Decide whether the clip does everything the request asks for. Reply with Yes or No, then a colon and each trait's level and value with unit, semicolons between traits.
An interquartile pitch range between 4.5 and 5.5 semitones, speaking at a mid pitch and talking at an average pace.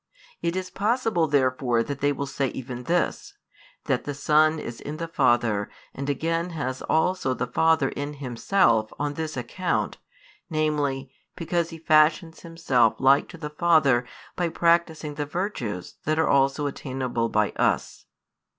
No: average, 4.0 semitones; medium, 145 Hz; average, 150 wpm